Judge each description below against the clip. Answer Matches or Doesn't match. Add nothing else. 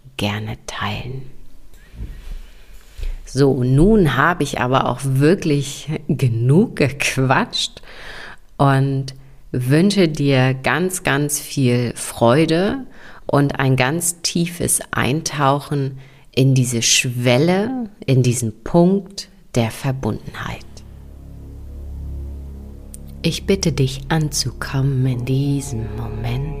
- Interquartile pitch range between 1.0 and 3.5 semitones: Doesn't match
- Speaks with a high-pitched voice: Doesn't match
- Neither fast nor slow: Doesn't match